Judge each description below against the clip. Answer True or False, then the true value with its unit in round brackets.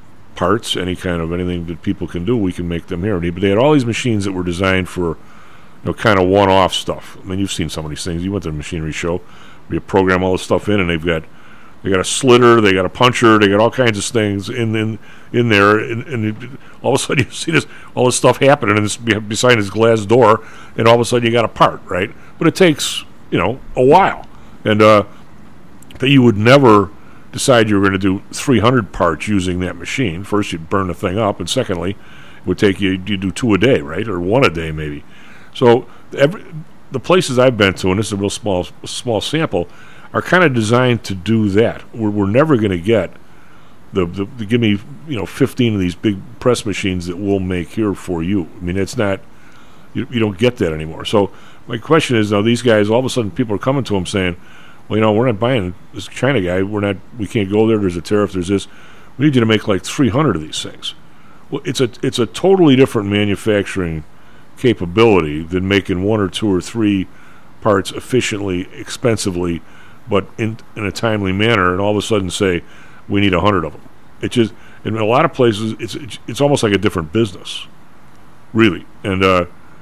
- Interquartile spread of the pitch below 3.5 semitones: False (3.9 semitones)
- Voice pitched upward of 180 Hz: False (105 Hz)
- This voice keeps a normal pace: False (230 wpm)